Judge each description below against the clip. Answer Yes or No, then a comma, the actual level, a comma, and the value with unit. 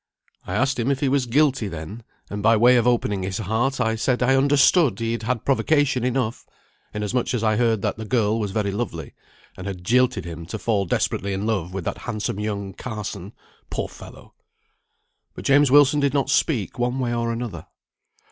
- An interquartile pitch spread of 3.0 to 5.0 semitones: Yes, average, 4.1 semitones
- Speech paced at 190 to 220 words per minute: Yes, average, 195 wpm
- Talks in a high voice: No, low, 115 Hz